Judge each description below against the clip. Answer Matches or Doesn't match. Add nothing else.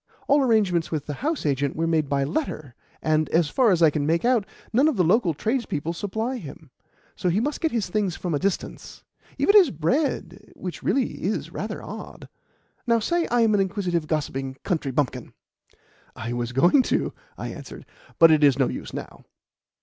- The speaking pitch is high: Doesn't match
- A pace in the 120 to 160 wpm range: Doesn't match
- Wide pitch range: Matches